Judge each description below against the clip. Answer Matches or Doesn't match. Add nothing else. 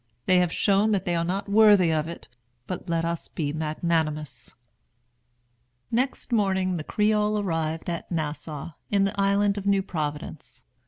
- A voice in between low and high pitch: Matches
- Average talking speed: Matches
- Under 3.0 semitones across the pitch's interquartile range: Doesn't match